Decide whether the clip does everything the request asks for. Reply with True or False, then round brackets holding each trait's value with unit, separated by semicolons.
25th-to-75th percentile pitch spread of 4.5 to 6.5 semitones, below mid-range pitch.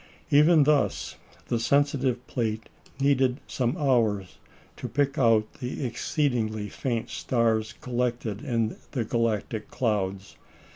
False (3.8 semitones; 120 Hz)